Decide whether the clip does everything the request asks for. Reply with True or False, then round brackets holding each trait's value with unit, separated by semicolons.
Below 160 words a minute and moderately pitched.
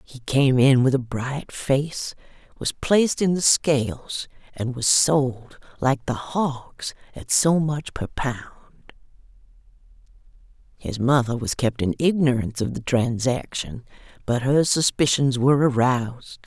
False (135 wpm; 130 Hz)